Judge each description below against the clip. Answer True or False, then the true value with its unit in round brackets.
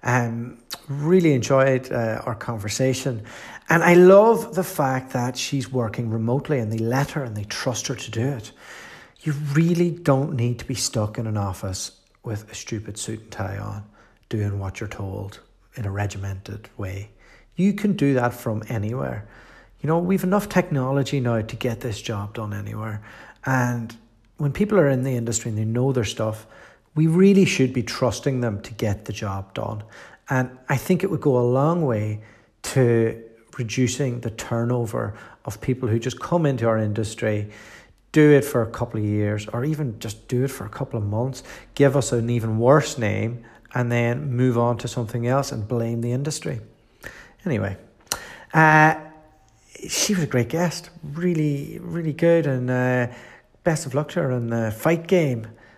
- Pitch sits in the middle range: False (120 Hz)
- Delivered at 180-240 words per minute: True (185 wpm)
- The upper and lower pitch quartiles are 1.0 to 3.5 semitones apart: False (4.2 semitones)